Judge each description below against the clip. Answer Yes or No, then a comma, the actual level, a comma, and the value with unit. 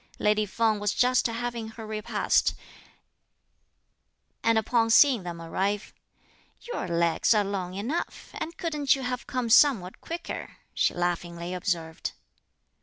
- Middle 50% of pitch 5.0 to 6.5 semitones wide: Yes, wide, 5.4 semitones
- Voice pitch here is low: No, high, 215 Hz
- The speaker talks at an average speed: No, slow, 125 wpm